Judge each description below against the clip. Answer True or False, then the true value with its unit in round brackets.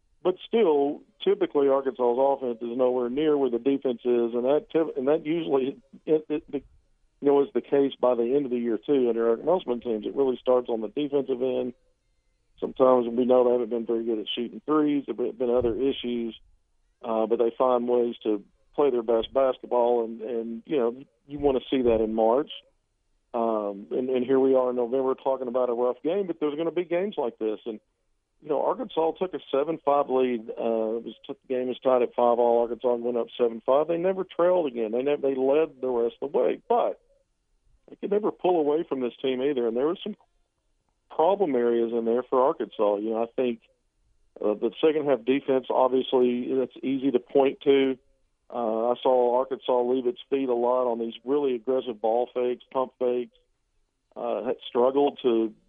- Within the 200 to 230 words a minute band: True (205 wpm)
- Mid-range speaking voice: False (125 Hz)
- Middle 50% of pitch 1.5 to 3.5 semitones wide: True (2.9 semitones)